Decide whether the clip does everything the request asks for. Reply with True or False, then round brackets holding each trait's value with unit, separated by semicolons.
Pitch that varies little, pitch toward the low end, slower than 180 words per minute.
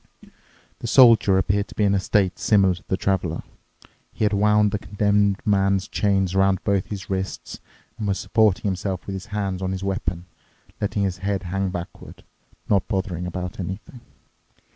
True (1.5 semitones; 95 Hz; 170 wpm)